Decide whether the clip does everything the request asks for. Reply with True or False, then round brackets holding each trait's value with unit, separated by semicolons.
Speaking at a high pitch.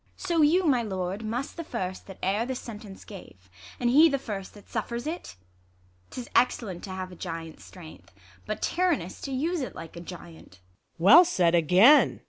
True (210 Hz)